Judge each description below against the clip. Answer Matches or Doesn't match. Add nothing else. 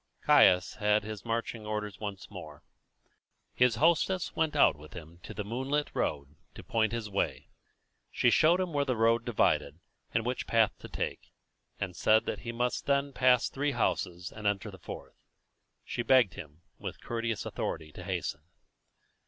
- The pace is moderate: Matches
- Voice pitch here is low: Matches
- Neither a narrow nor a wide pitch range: Matches